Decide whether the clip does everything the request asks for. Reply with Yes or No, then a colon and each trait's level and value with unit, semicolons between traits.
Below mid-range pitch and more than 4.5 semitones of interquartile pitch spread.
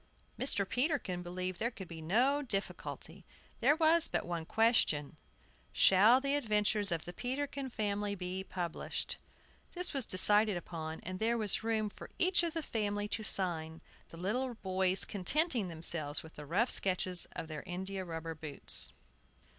No: high, 200 Hz; average, 5.3 semitones